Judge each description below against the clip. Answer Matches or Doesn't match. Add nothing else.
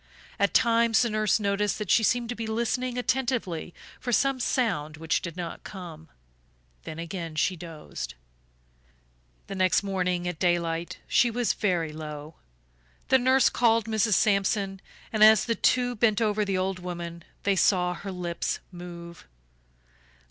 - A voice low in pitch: Doesn't match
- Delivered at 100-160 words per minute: Matches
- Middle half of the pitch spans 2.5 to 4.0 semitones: Doesn't match